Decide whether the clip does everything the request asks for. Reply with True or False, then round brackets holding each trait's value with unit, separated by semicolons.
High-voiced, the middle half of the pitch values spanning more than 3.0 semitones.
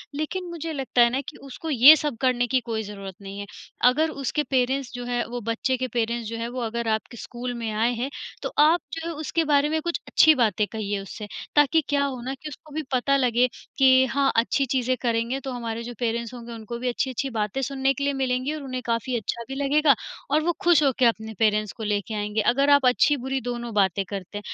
True (250 Hz; 3.4 semitones)